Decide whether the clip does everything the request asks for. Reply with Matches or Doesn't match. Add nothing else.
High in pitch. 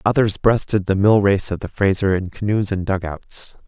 Doesn't match